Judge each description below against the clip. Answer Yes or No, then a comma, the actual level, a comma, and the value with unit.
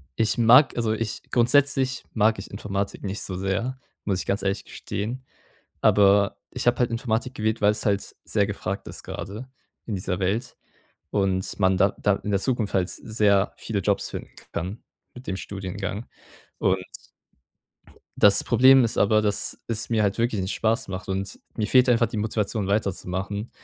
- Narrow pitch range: No, average, 3.0 semitones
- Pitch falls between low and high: No, low, 105 Hz